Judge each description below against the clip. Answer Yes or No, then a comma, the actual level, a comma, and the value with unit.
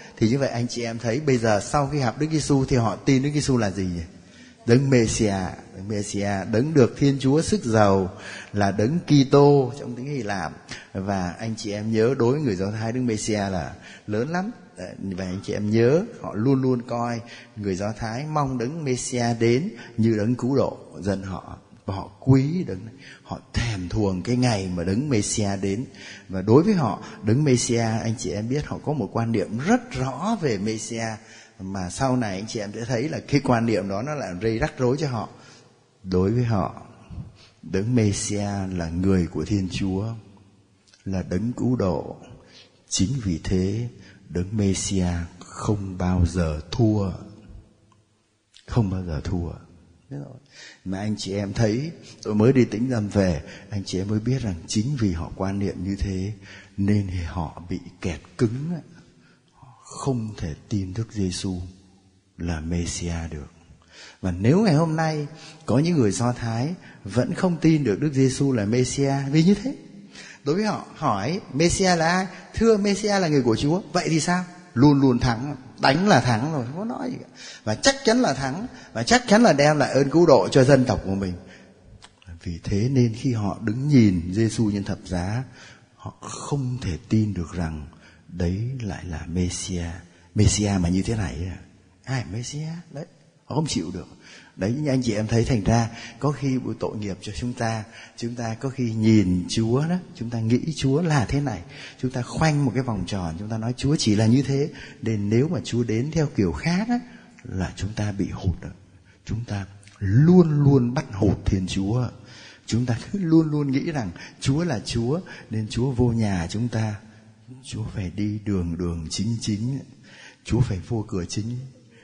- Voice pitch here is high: No, low, 110 Hz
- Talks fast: No, average, 190 wpm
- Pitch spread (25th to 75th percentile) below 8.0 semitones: Yes, wide, 5.5 semitones